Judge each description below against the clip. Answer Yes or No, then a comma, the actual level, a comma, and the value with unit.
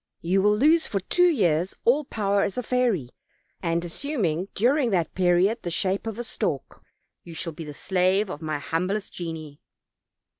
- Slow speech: No, average, 175 wpm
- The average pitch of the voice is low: No, high, 190 Hz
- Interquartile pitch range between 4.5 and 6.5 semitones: Yes, average, 5.2 semitones